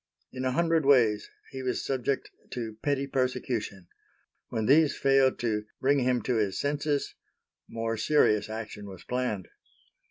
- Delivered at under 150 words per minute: Yes, average, 140 wpm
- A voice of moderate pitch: No, low, 125 Hz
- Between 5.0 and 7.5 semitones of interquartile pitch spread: No, average, 3.8 semitones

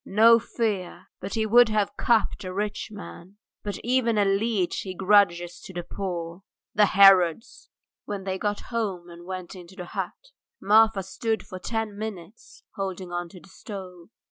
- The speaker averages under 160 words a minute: No, average, 170 wpm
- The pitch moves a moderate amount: Yes, average, 3.0 semitones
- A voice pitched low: No, high, 195 Hz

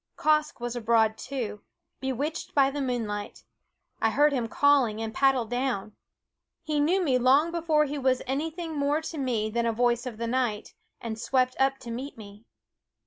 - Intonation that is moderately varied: Yes, average, 3.9 semitones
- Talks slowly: No, average, 180 wpm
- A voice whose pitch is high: Yes, very high, 255 Hz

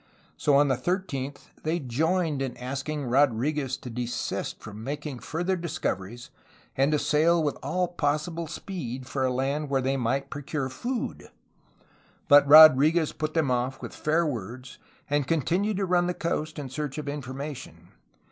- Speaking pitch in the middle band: Yes, medium, 145 Hz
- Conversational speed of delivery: Yes, average, 155 wpm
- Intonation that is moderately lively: Yes, average, 3.5 semitones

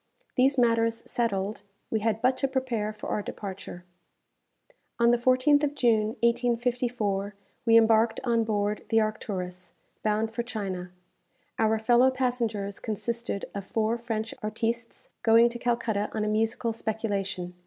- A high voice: Yes, high, 225 Hz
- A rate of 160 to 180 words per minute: No, average, 140 wpm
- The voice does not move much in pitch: Yes, narrow, 2.1 semitones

